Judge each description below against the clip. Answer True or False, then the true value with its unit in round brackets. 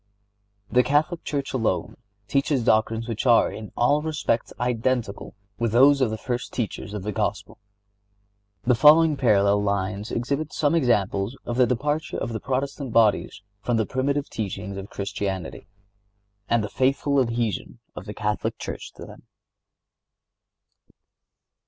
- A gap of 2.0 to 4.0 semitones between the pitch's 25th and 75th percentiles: False (4.6 semitones)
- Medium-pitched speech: False (120 Hz)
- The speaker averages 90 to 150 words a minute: True (140 wpm)